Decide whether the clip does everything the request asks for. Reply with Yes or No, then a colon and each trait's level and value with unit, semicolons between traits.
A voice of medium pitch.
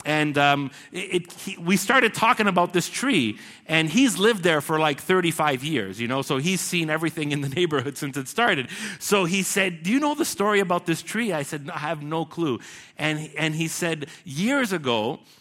Yes: medium, 170 Hz